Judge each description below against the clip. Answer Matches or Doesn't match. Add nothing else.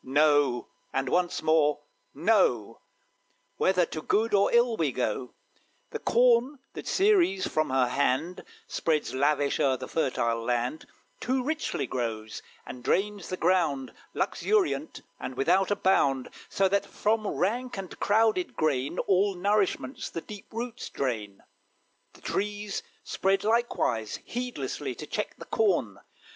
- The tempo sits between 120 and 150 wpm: Matches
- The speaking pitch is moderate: Matches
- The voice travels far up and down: Matches